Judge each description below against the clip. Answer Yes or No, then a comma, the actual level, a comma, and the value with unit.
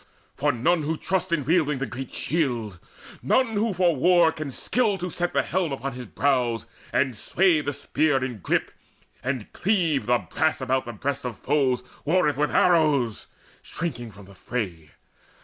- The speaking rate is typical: Yes, average, 170 wpm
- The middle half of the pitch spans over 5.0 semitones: Yes, wide, 5.4 semitones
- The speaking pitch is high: No, medium, 140 Hz